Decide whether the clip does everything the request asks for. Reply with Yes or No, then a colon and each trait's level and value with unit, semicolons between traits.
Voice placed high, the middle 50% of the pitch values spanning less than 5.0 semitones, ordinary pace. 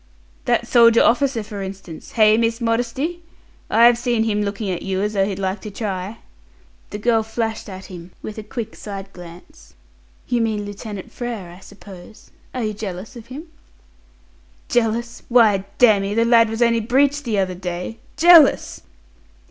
Yes: high, 220 Hz; average, 3.2 semitones; average, 165 wpm